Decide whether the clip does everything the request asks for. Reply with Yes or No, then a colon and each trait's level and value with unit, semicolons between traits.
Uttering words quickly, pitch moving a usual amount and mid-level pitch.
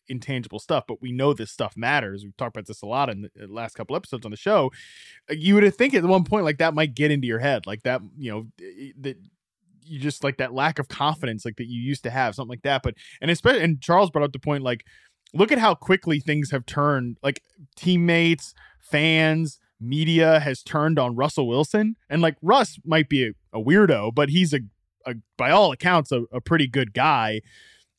Yes: fast, 220 wpm; average, 4.7 semitones; medium, 145 Hz